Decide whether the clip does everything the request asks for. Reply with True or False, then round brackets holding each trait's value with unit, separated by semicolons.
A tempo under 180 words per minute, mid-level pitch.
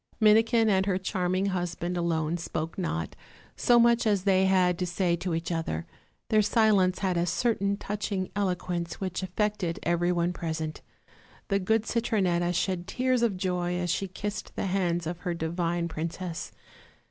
True (160 wpm; 180 Hz)